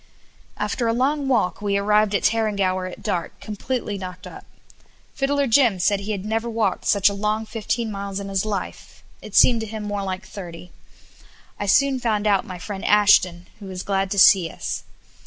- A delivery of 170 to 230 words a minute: Yes, average, 190 wpm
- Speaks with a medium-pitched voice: No, high, 205 Hz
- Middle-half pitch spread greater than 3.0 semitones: No, narrow, 2.5 semitones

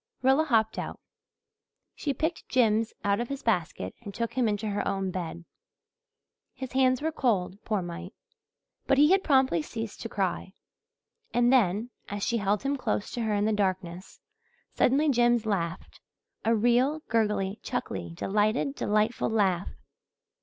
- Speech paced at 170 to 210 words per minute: No, average, 155 wpm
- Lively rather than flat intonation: No, average, 4.6 semitones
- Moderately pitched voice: No, high, 220 Hz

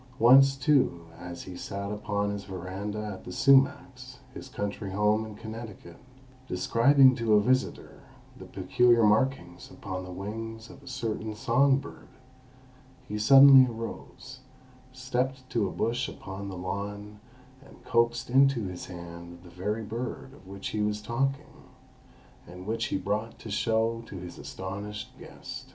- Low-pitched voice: Yes, low, 110 Hz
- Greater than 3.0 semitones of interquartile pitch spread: Yes, average, 4.4 semitones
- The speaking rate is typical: Yes, average, 150 wpm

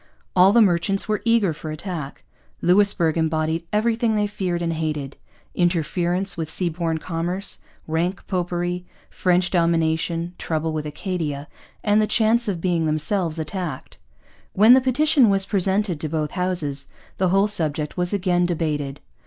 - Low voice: No, medium, 175 Hz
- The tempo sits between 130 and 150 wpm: Yes, average, 145 wpm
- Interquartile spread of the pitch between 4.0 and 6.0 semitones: No, average, 3.5 semitones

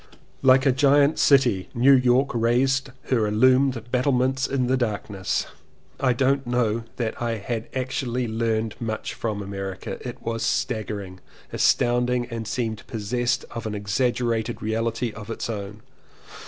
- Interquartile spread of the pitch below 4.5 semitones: Yes, average, 2.7 semitones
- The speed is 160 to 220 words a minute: No, average, 140 wpm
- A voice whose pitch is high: No, low, 120 Hz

